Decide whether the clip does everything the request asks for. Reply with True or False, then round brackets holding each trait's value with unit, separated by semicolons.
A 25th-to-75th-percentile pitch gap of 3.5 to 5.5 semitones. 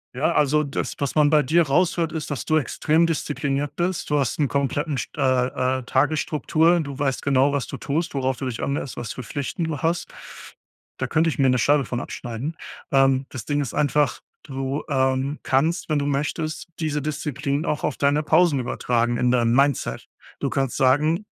False (2.5 semitones)